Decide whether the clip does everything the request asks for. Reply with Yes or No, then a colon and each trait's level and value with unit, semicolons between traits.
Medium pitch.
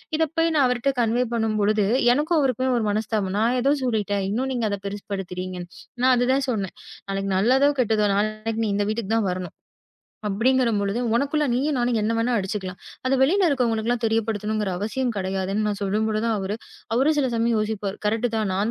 No: high, 220 Hz